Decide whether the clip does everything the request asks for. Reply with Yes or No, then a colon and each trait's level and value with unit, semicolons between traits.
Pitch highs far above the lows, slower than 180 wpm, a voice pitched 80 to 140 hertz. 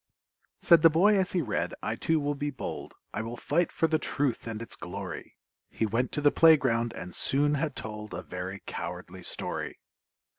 No: wide, 6.4 semitones; average, 190 wpm; low, 135 Hz